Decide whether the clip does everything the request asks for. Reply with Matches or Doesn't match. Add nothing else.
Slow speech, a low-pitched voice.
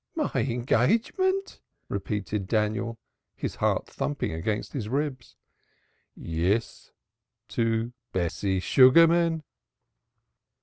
Matches